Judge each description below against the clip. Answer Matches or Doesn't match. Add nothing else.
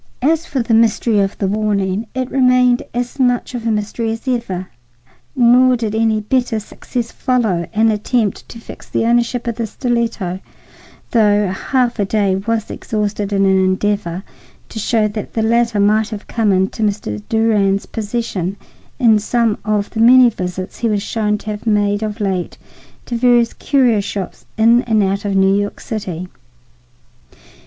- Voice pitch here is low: Doesn't match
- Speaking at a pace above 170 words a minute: Doesn't match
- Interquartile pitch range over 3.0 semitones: Doesn't match